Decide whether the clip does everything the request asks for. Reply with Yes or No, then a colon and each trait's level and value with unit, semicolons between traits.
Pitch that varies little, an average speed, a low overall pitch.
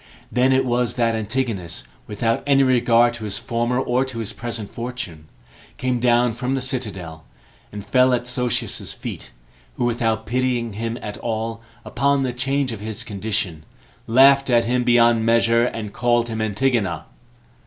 Yes: narrow, 2.1 semitones; average, 160 wpm; low, 120 Hz